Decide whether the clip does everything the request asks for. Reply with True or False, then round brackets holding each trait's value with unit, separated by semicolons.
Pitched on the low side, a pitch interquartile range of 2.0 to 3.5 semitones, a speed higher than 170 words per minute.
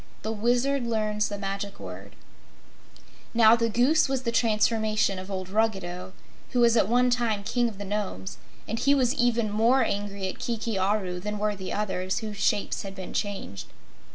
False (210 Hz; 3.1 semitones; 180 wpm)